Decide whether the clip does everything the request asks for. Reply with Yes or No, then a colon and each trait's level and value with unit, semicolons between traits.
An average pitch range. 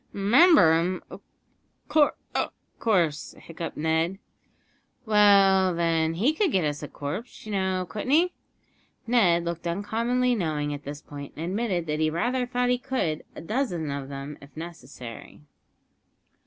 No: wide, 6.1 semitones